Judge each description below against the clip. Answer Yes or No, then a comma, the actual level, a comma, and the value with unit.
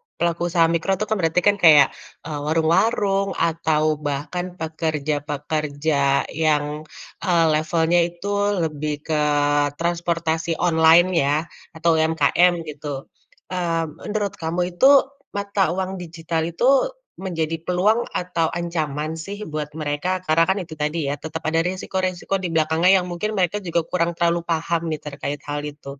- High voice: No, medium, 165 Hz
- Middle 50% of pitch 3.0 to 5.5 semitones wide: No, narrow, 2.5 semitones